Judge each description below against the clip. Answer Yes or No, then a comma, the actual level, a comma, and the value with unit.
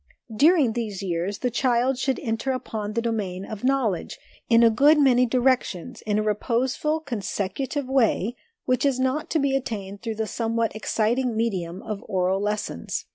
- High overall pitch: Yes, high, 230 Hz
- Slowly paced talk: No, average, 165 wpm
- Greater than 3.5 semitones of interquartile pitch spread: Yes, average, 3.9 semitones